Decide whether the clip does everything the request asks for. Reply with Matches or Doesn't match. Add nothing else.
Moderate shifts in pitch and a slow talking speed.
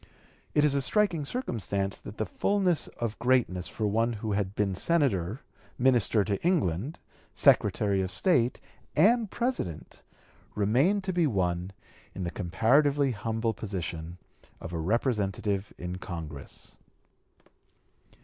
Doesn't match